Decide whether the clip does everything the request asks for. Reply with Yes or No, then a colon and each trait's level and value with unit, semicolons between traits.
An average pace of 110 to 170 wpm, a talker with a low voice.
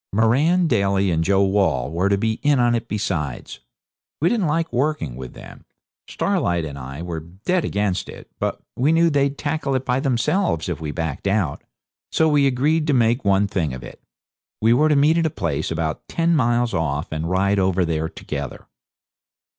No: average, 185 wpm; low, 105 Hz